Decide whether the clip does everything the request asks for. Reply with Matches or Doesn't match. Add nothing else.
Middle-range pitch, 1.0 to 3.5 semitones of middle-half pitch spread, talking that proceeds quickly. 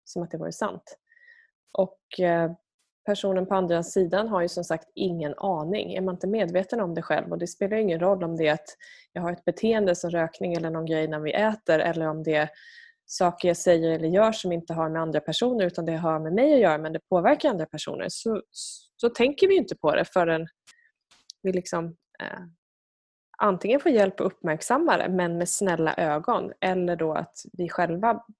Doesn't match